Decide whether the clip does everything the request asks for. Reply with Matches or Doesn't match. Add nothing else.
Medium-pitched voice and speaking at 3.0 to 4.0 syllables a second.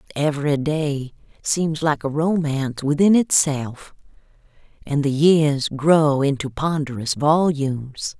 Matches